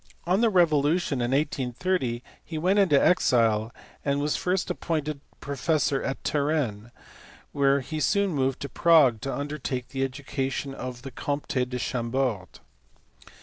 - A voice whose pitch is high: No, medium, 140 Hz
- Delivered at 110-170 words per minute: Yes, average, 140 wpm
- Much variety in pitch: No, average, 3.4 semitones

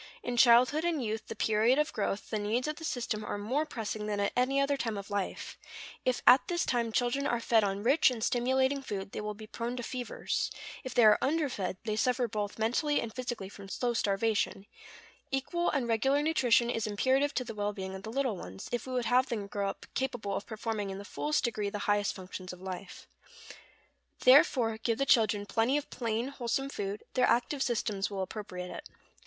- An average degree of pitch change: Yes, average, 3.9 semitones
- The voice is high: Yes, high, 230 Hz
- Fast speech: Yes, fast, 210 wpm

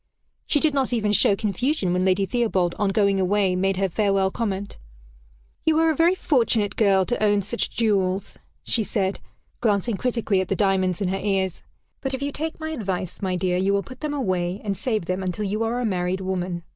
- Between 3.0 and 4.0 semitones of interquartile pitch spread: Yes, average, 3.7 semitones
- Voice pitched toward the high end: Yes, high, 200 Hz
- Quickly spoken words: Yes, fast, 210 wpm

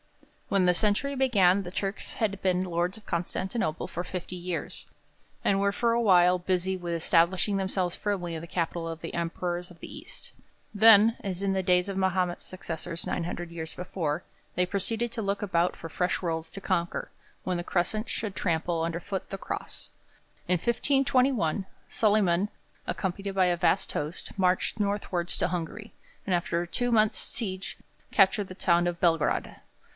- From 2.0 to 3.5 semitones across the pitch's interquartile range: Yes, narrow, 2.6 semitones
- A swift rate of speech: No, average, 170 wpm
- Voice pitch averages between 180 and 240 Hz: Yes, medium, 185 Hz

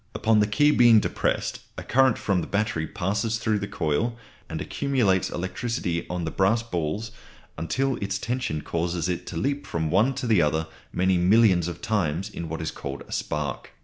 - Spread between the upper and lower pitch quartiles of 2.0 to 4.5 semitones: No, average, 5.3 semitones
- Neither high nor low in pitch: No, low, 100 Hz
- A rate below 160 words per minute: No, average, 185 wpm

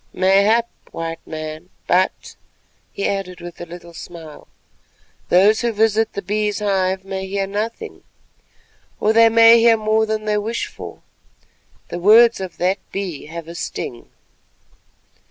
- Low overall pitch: No, high, 195 Hz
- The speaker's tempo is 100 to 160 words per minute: Yes, average, 140 wpm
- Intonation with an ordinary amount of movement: Yes, average, 3.7 semitones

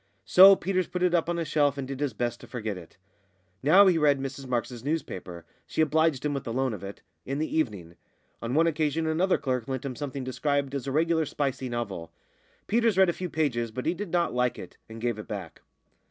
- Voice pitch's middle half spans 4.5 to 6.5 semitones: Yes, average, 5.1 semitones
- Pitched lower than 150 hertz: Yes, medium, 140 Hz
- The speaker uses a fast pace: Yes, fast, 225 wpm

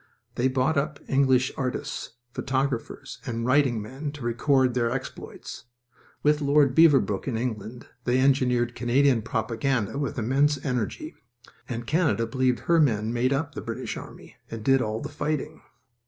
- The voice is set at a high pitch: No, low, 130 Hz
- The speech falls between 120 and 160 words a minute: Yes, average, 150 wpm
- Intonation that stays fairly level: No, average, 3.0 semitones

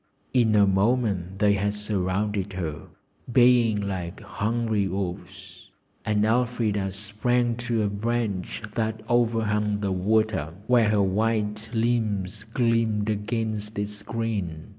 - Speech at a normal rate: No, slow, 120 wpm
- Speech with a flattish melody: Yes, narrow, 2.2 semitones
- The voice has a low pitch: Yes, low, 105 Hz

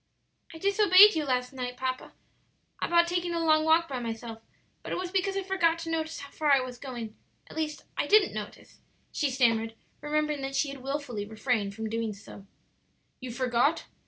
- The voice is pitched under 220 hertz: No, very high, 275 Hz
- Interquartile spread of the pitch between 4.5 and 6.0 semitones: Yes, wide, 5.5 semitones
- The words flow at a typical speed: Yes, average, 190 wpm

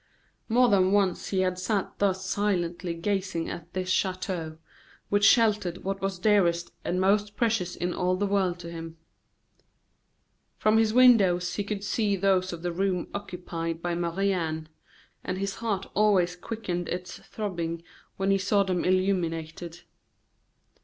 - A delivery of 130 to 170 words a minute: Yes, average, 150 wpm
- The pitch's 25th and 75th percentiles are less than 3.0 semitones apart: Yes, narrow, 2.5 semitones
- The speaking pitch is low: No, medium, 185 Hz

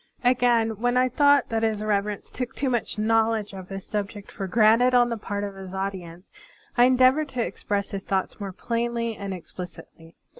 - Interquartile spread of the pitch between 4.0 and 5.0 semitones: No, average, 3.5 semitones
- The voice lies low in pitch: No, high, 215 Hz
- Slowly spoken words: No, average, 190 wpm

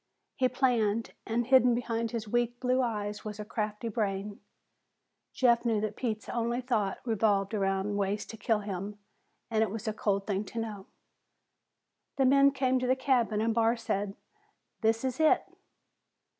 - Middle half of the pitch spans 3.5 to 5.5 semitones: No, average, 2.7 semitones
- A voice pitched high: Yes, high, 225 Hz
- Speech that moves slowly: No, average, 165 wpm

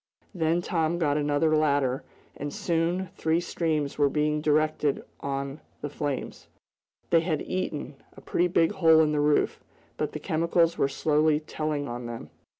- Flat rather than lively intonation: Yes, narrow, 2.2 semitones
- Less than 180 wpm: Yes, average, 155 wpm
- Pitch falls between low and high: Yes, medium, 155 Hz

